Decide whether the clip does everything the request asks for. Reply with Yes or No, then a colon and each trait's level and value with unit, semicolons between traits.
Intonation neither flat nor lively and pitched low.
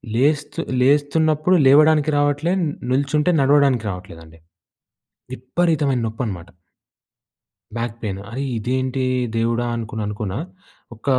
Yes: average, 4.5 semitones; low, 130 Hz